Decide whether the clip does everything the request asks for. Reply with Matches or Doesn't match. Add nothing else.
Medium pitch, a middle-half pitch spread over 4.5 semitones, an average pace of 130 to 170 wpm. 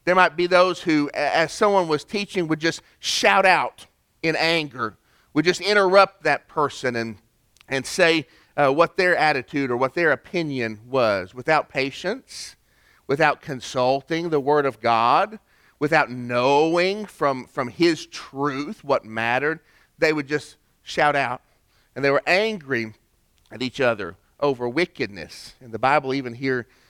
Matches